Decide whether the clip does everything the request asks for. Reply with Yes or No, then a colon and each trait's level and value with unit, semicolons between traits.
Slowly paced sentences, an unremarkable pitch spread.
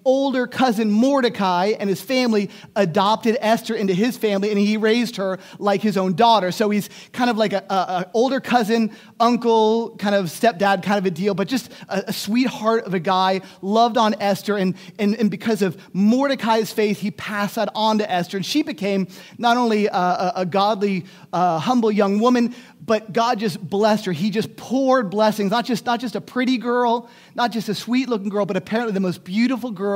No: average, 200 wpm; average, 3.0 semitones